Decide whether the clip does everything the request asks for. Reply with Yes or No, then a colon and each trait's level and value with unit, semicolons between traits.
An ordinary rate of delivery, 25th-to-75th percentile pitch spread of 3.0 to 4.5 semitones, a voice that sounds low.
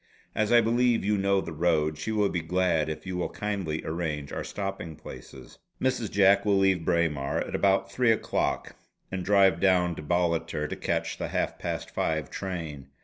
Yes: average, 185 wpm; average, 3.8 semitones; very low, 90 Hz